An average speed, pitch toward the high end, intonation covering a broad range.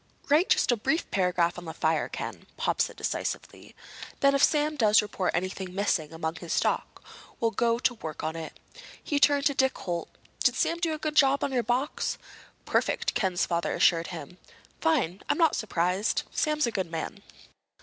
Yes: average, 185 wpm; high, 210 Hz; wide, 8.3 semitones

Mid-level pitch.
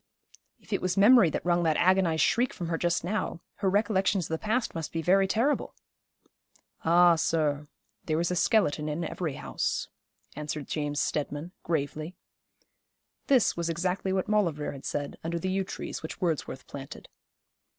Yes: medium, 170 Hz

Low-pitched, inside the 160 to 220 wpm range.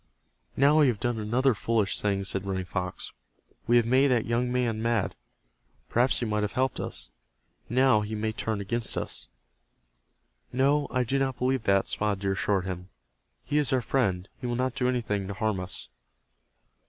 Yes: low, 115 Hz; average, 180 wpm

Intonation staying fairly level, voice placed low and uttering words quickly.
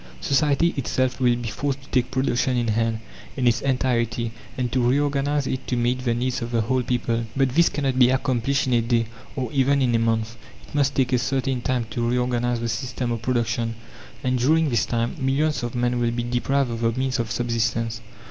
Yes: narrow, 2.1 semitones; low, 125 Hz; fast, 215 wpm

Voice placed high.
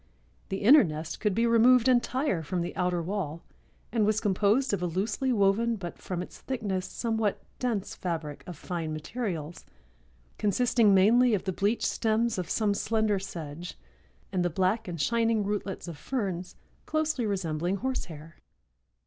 Yes: high, 200 Hz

